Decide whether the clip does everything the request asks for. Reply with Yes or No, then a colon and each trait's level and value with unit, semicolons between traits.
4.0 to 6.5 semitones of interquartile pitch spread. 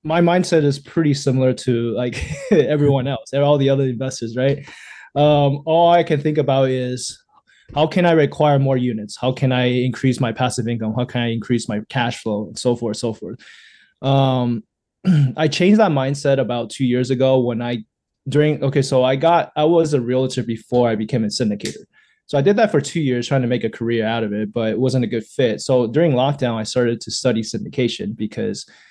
No: average, 3.2 semitones